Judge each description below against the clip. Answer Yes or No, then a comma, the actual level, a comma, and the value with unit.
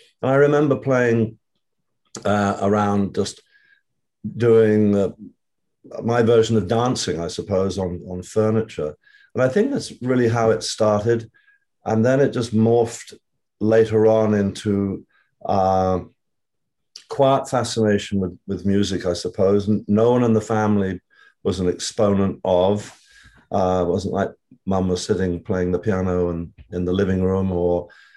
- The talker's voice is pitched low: Yes, low, 105 Hz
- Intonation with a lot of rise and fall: No, average, 3.7 semitones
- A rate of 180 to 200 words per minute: No, average, 145 wpm